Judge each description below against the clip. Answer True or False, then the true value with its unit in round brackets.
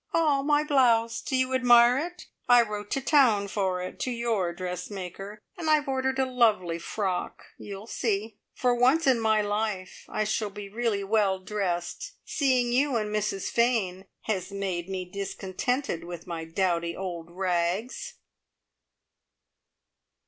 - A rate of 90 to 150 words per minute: True (145 wpm)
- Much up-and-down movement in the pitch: False (5.0 semitones)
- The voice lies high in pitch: True (210 Hz)